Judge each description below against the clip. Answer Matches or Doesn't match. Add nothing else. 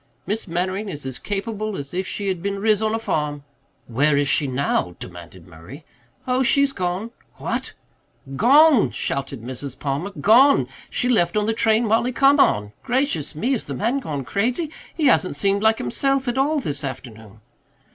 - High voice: Matches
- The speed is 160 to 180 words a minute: Matches